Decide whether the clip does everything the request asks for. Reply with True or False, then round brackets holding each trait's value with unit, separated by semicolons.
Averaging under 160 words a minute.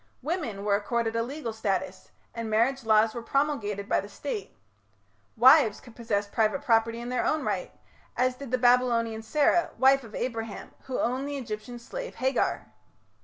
False (170 wpm)